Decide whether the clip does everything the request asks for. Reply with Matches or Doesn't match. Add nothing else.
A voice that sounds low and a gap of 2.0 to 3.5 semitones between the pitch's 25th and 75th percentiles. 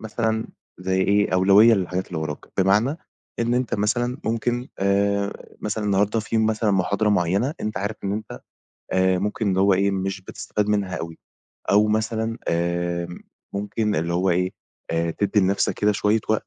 Matches